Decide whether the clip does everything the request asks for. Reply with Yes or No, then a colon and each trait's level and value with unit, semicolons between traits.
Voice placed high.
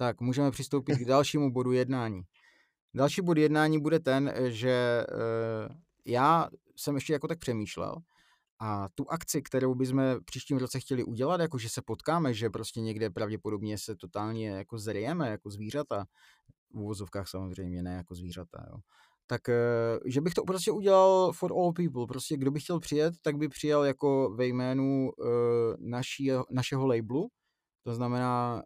No: low, 130 Hz